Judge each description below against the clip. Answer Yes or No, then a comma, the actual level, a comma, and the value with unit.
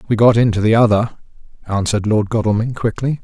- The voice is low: Yes, low, 110 Hz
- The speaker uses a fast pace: No, average, 165 wpm